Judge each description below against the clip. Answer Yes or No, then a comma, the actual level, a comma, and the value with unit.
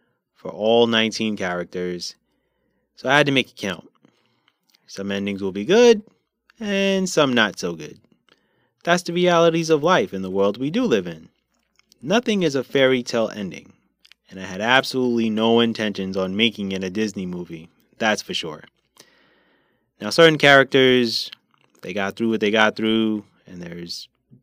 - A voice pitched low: Yes, low, 115 Hz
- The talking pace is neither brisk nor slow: Yes, average, 160 wpm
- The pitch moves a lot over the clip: Yes, wide, 6.9 semitones